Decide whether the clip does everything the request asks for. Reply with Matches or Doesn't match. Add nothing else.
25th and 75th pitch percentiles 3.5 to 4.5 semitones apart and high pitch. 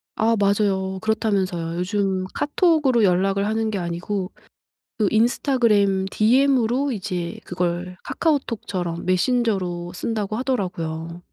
Matches